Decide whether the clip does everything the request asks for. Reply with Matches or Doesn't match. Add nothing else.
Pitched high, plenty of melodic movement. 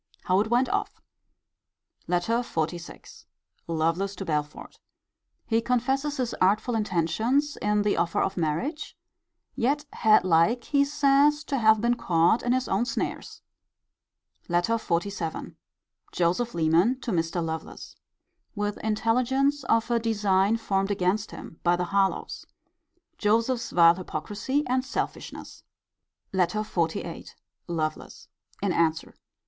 Matches